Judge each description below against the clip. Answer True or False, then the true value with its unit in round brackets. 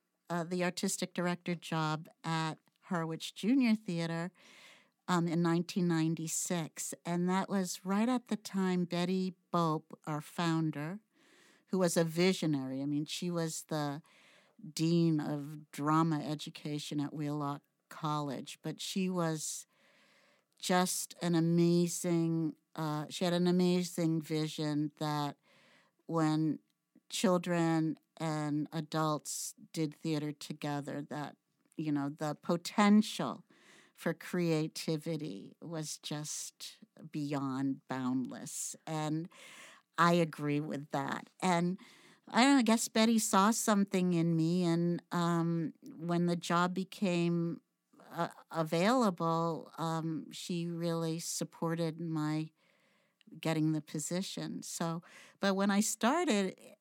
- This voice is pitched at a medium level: True (170 Hz)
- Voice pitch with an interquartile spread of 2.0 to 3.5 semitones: True (2.9 semitones)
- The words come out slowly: True (110 wpm)